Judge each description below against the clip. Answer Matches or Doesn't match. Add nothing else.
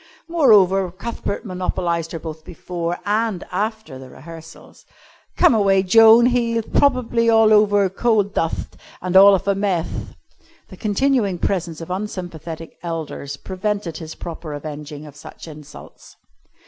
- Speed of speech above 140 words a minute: Doesn't match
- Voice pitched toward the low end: Doesn't match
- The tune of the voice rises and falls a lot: Doesn't match